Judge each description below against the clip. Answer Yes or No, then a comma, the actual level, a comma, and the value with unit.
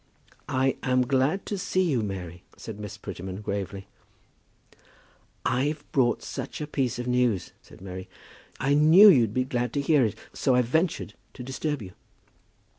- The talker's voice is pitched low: Yes, low, 125 Hz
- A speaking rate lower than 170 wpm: Yes, average, 160 wpm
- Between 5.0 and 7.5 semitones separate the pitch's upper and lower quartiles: Yes, wide, 5.6 semitones